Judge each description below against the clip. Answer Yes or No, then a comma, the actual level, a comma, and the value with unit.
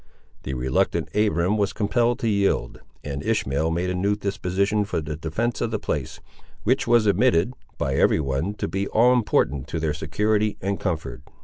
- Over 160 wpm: Yes, average, 180 wpm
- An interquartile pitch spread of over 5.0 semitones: Yes, wide, 5.4 semitones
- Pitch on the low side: Yes, low, 100 Hz